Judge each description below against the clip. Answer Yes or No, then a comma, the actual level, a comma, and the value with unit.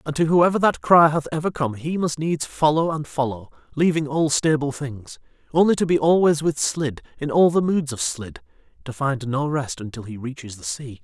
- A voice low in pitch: No, medium, 145 Hz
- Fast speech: Yes, fast, 210 wpm